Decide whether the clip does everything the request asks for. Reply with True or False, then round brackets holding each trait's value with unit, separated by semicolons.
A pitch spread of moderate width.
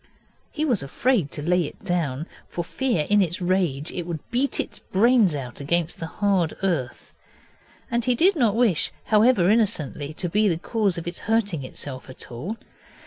False (6.1 semitones)